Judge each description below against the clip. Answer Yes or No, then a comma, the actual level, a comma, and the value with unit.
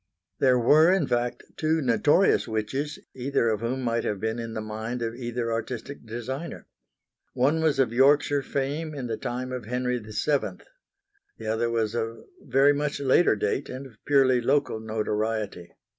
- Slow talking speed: No, average, 165 wpm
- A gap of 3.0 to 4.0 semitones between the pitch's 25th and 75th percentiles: Yes, average, 3.7 semitones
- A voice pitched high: No, low, 125 Hz